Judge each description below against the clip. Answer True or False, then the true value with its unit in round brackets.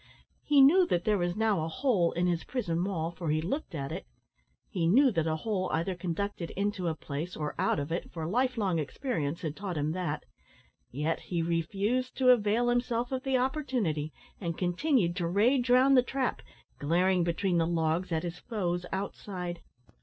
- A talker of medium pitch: True (180 Hz)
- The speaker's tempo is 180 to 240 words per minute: True (190 wpm)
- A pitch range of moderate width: False (6.4 semitones)